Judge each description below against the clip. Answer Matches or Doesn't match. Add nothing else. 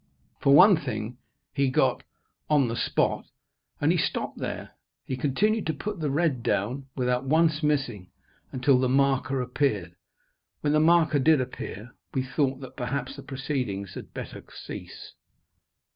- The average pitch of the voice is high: Doesn't match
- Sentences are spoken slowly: Doesn't match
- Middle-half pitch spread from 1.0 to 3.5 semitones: Matches